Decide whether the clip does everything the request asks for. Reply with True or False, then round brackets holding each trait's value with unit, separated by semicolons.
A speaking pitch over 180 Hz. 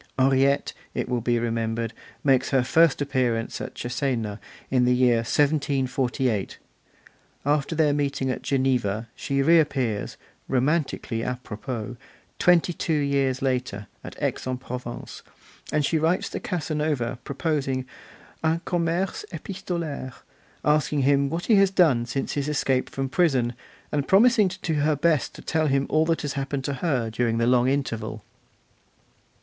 False (135 Hz)